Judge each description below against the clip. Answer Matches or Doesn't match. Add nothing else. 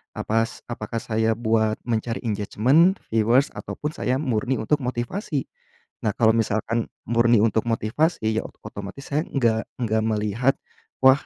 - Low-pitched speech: Matches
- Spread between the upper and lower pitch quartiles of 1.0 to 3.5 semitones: Matches